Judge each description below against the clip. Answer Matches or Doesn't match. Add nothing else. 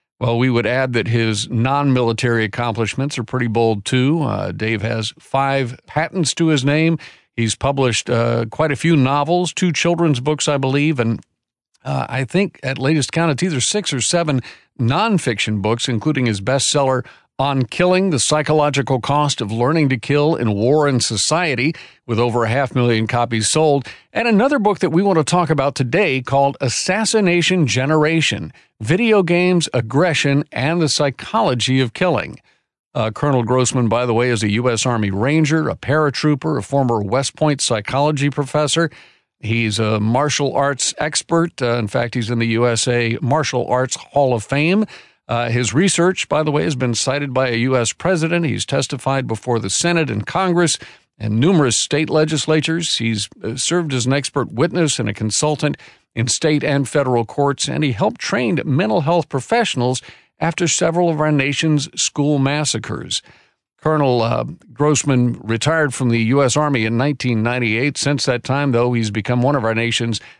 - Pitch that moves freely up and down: Doesn't match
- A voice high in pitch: Doesn't match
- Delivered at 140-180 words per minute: Matches